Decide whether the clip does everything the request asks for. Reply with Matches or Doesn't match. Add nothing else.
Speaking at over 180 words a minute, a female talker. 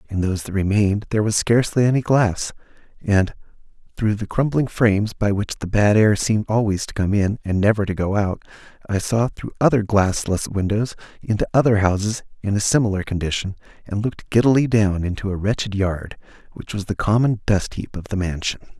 Doesn't match